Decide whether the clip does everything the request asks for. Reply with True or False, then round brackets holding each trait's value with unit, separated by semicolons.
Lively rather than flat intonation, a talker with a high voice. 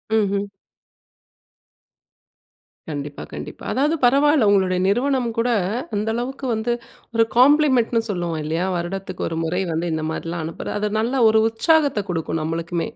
True (6.4 semitones; 205 Hz)